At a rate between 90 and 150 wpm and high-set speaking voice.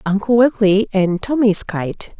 Yes: slow, 135 wpm; high, 205 Hz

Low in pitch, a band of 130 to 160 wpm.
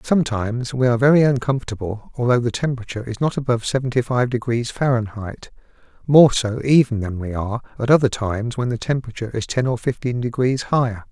No: low, 120 Hz; average, 180 wpm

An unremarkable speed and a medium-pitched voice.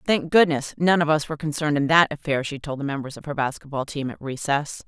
No: fast, 245 wpm; medium, 150 Hz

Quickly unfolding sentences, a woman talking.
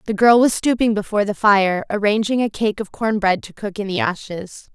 Yes: fast, 230 wpm; female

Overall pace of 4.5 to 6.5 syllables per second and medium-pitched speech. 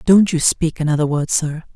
Yes: 5.1 syllables/s; medium, 160 Hz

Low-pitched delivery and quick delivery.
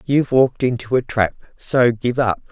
No: low, 125 Hz; average, 190 wpm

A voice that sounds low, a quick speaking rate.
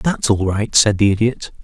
Yes: low, 105 Hz; fast, 220 wpm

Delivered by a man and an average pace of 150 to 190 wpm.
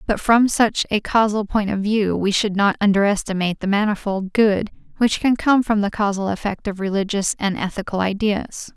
No: female; average, 185 wpm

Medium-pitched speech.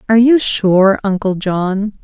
No: high, 205 Hz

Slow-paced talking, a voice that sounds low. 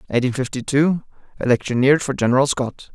Yes: slow, 120 wpm; low, 130 Hz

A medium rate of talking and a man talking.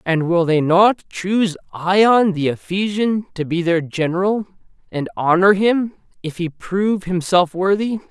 Yes: average, 150 wpm; male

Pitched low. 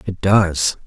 Yes: very low, 90 Hz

